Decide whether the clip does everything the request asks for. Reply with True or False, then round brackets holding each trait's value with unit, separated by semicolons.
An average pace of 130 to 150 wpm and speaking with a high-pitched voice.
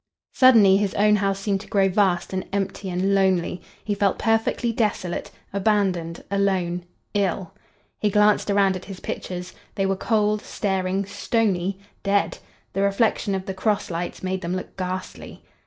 True (145 wpm; 195 Hz)